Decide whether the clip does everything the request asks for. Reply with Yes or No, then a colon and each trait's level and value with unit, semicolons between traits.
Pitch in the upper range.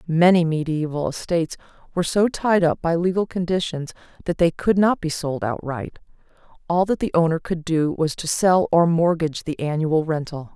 No: medium, 165 Hz